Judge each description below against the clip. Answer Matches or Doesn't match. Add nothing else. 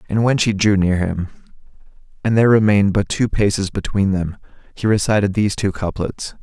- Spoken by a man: Matches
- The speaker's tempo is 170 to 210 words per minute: Matches